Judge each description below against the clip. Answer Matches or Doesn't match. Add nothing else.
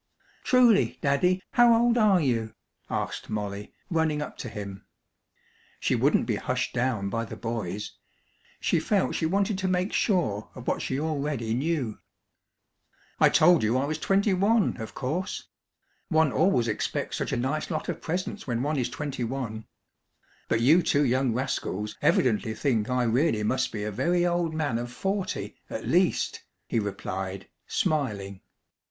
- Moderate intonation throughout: Doesn't match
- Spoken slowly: Doesn't match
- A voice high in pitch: Doesn't match